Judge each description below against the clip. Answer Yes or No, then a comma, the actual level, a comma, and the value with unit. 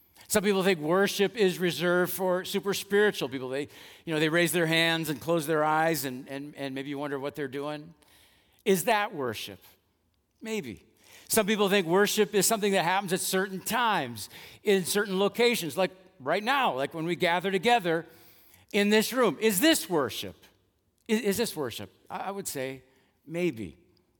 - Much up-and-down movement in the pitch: Yes, wide, 5.7 semitones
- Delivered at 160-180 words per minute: Yes, average, 175 wpm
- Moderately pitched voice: Yes, medium, 175 Hz